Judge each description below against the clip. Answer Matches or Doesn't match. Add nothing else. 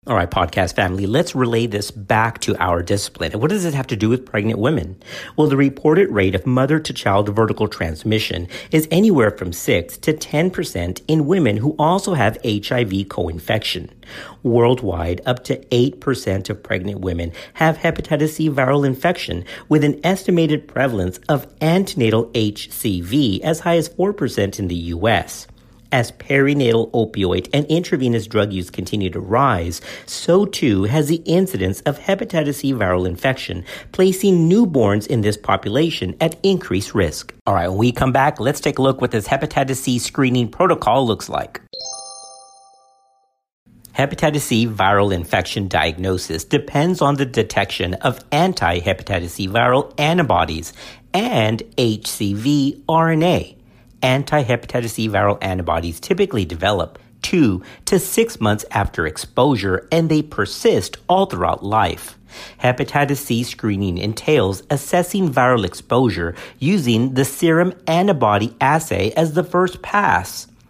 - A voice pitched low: Matches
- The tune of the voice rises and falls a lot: Matches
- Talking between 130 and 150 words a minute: Matches